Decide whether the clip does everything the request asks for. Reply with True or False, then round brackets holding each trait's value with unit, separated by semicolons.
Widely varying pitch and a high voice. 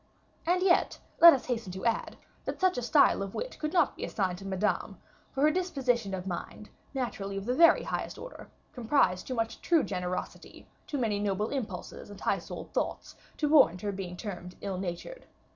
True (7.1 semitones; 225 Hz)